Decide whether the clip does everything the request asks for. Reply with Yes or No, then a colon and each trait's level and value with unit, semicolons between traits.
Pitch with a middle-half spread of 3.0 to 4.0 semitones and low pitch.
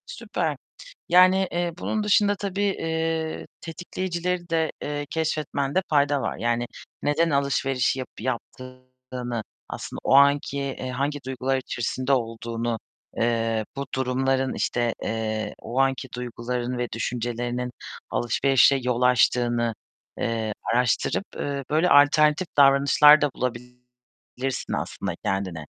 Yes: average, 3.5 semitones; low, 130 Hz